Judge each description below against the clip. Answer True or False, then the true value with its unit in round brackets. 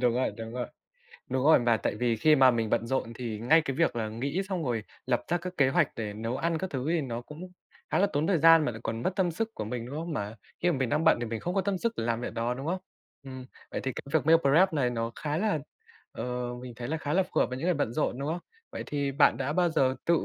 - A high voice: False (135 Hz)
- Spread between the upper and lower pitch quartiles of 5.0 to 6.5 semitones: True (5.4 semitones)